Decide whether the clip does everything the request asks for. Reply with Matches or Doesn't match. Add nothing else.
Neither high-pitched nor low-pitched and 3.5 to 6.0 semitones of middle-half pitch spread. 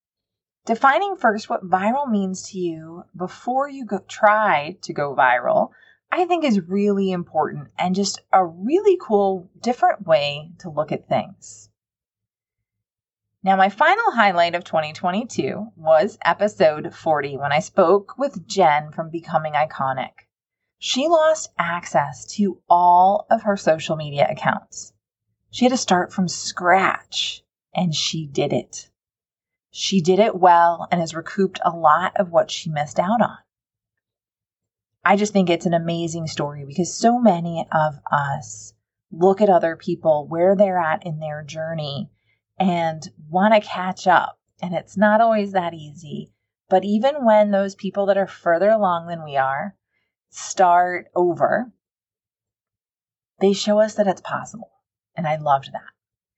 Matches